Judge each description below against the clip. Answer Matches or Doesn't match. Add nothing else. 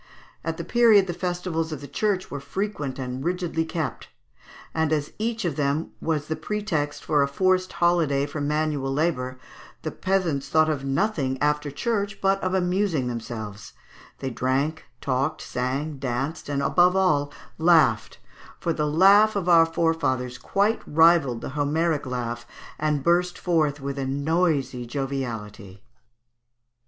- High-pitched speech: Doesn't match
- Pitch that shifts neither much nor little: Matches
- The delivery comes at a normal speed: Matches